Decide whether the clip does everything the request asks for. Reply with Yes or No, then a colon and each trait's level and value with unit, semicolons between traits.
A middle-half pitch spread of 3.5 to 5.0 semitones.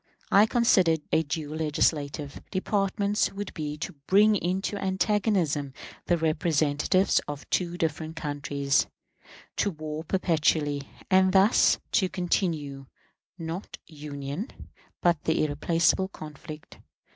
Yes: average, 4.2 semitones